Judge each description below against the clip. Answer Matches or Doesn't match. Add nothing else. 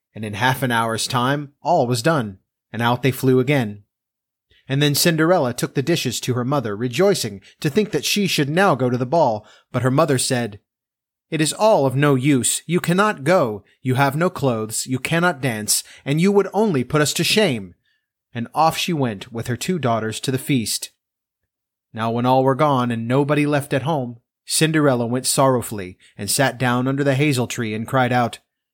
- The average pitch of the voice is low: Matches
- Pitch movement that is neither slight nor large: Matches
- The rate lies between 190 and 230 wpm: Matches